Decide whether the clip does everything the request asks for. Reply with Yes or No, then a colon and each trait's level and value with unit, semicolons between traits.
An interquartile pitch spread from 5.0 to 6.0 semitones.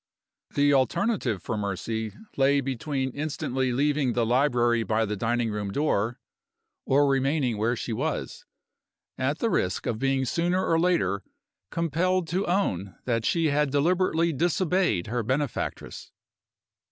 Yes: wide, 5.6 semitones